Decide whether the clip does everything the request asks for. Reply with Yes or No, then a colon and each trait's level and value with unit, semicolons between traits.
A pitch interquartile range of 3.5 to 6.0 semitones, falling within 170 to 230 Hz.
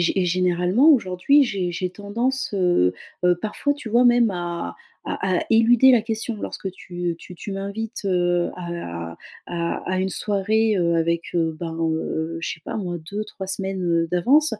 Yes: average, 4.1 semitones; medium, 185 Hz